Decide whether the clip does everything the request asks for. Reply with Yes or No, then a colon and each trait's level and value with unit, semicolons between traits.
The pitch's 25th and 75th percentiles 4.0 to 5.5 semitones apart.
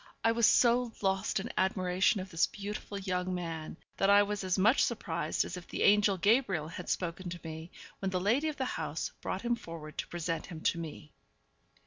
No: average, 3.5 semitones